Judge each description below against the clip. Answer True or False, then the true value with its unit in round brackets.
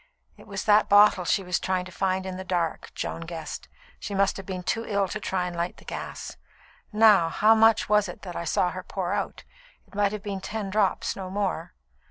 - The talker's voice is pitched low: False (190 Hz)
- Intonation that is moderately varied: False (2.3 semitones)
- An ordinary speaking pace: False (225 wpm)